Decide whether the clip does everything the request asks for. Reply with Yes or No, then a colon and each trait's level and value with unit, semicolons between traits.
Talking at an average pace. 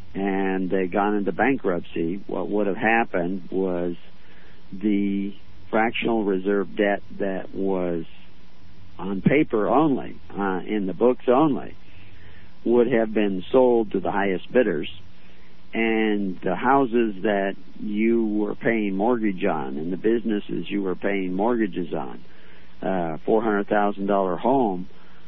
No: slow, 130 wpm